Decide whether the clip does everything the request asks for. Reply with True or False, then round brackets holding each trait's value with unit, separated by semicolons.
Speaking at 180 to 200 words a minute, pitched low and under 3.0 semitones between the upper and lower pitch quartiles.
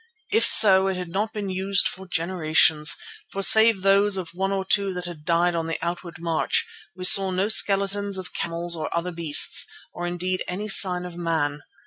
False (190 wpm; 185 Hz; 2.5 semitones)